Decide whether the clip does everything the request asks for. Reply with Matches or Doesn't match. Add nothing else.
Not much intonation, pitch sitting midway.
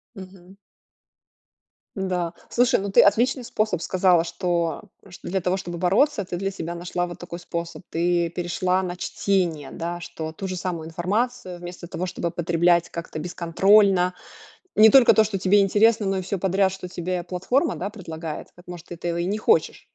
Matches